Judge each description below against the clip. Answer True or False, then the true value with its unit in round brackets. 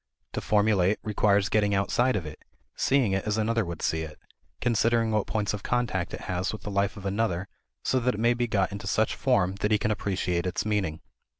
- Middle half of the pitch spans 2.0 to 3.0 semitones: True (2.6 semitones)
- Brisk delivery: True (215 wpm)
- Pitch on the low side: True (105 Hz)